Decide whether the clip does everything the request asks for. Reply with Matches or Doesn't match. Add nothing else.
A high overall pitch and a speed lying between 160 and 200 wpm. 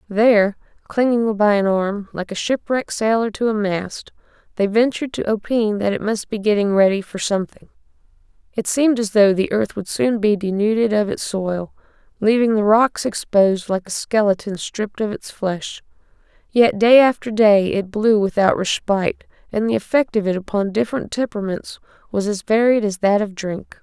Matches